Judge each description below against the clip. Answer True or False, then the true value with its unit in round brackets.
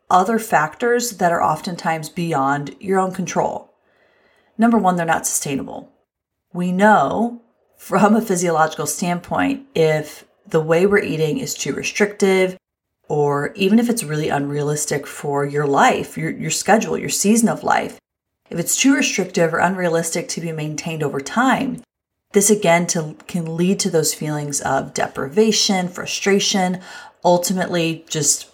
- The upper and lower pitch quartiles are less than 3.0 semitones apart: False (4.4 semitones)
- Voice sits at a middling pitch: True (175 Hz)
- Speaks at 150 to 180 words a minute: False (140 wpm)